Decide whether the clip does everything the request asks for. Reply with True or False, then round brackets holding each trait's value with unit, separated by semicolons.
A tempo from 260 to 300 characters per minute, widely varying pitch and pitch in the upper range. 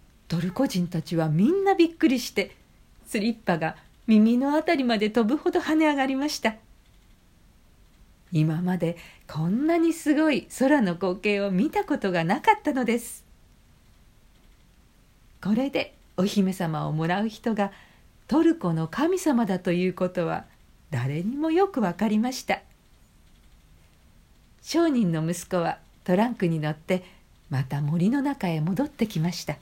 True (265 characters per minute; 8.4 semitones; 195 Hz)